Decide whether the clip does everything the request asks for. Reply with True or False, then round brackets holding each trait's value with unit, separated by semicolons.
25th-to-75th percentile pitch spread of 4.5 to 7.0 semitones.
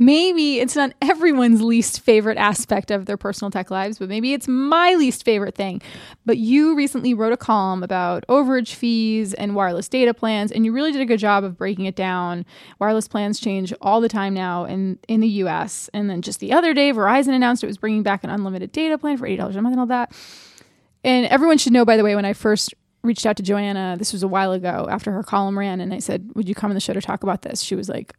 False (4.1 semitones)